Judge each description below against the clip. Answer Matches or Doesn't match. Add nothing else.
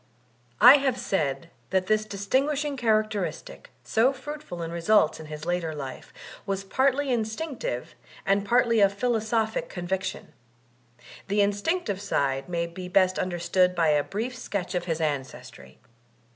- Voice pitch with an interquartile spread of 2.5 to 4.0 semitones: Doesn't match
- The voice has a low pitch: Doesn't match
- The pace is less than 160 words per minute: Matches